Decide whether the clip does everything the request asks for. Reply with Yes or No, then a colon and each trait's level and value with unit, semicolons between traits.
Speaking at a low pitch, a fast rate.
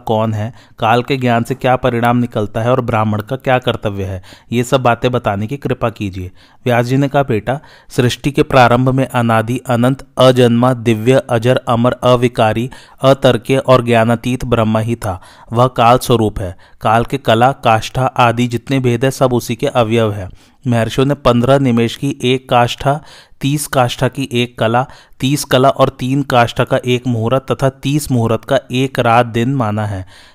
No: low, 125 Hz; average, 180 wpm